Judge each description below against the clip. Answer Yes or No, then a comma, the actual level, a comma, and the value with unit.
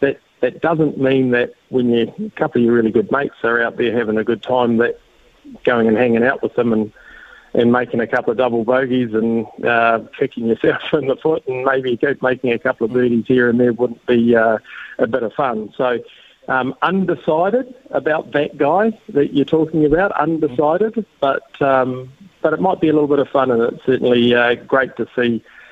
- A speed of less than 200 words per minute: No, fast, 205 wpm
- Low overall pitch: Yes, low, 130 Hz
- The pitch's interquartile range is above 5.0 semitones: No, average, 4.4 semitones